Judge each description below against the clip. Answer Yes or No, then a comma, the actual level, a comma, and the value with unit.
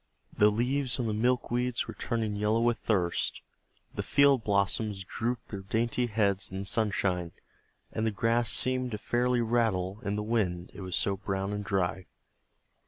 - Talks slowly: No, average, 170 wpm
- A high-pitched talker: No, low, 110 Hz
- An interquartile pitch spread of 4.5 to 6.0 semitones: No, average, 3.4 semitones